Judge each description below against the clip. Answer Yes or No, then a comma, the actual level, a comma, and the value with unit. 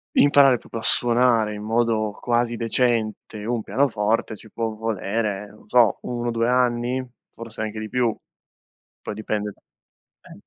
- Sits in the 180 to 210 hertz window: No, low, 115 Hz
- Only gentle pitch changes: Yes, narrow, 1.9 semitones